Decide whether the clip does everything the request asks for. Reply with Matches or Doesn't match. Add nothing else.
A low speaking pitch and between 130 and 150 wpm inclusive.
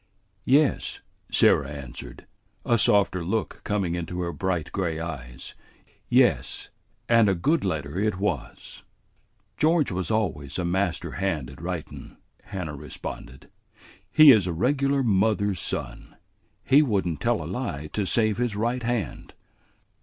Matches